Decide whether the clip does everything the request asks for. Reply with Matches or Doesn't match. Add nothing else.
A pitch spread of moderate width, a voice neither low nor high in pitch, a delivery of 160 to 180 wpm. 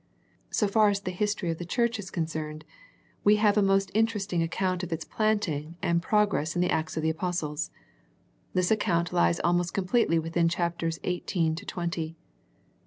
Matches